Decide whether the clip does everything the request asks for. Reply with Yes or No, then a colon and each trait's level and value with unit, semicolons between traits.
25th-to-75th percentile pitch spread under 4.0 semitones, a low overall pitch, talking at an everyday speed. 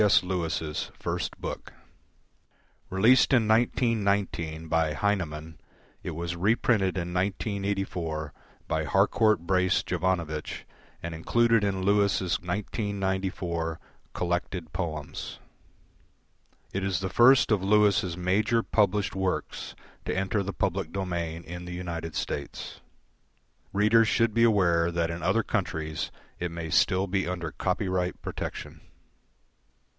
No: average, 3.2 semitones; very low, 95 Hz; slow, 115 wpm